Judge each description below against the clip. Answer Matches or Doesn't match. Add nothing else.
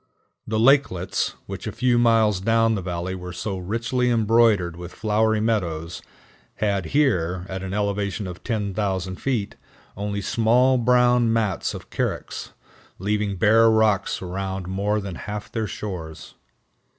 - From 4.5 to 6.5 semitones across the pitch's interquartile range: Doesn't match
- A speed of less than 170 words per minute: Matches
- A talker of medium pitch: Doesn't match